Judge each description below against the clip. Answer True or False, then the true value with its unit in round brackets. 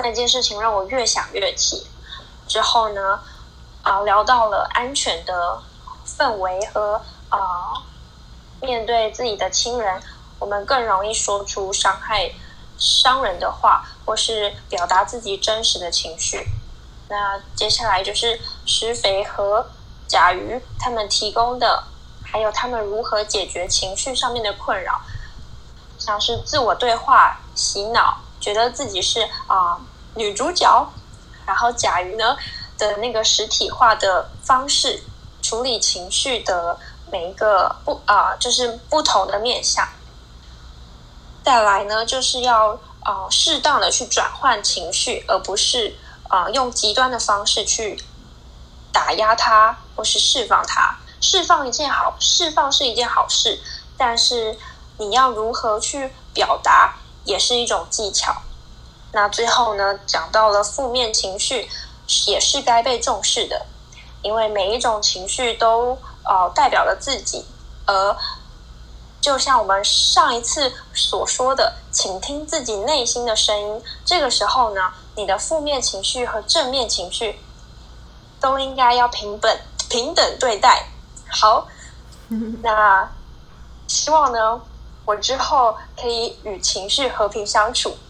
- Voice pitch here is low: False (220 Hz)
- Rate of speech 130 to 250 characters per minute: True (200 characters per minute)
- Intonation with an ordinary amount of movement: True (3.9 semitones)